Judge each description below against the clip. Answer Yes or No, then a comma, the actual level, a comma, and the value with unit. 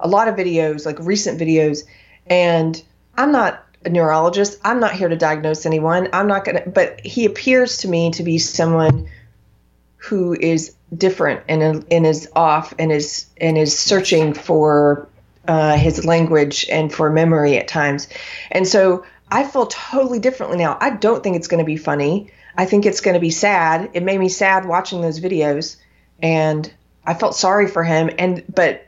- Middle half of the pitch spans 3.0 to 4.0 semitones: Yes, average, 3.3 semitones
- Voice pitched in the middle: Yes, medium, 165 Hz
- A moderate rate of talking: Yes, average, 180 wpm